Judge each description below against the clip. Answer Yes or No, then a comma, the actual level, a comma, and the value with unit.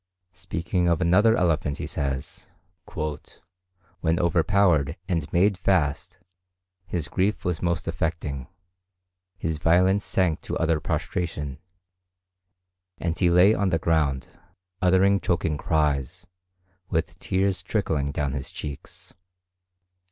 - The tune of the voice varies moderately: Yes, average, 3.3 semitones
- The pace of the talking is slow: Yes, slow, 110 wpm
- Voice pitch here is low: Yes, very low, 85 Hz